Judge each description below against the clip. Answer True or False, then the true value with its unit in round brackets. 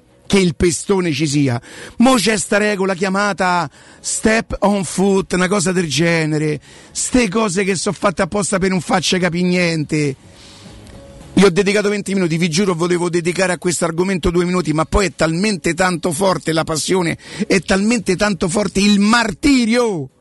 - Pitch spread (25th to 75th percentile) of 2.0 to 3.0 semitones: False (3.7 semitones)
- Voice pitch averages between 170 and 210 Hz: True (185 Hz)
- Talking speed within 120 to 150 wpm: False (165 wpm)